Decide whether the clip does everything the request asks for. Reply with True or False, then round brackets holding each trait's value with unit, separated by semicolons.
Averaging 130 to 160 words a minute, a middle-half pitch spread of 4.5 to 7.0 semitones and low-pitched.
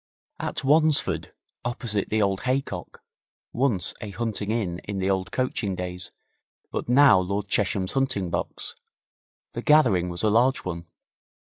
True (140 wpm; 5.2 semitones; 105 Hz)